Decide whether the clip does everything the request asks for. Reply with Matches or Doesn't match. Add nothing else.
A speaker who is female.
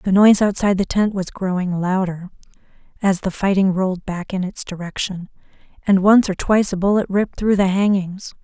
Matches